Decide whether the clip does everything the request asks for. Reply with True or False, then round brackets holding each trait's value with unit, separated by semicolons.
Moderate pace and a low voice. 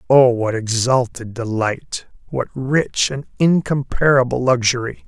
False (95 wpm; 125 Hz)